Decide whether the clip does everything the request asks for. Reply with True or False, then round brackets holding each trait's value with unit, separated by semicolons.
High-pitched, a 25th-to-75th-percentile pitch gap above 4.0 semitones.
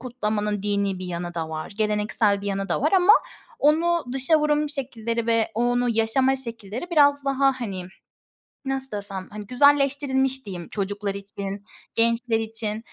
True (230 Hz; 4.9 semitones)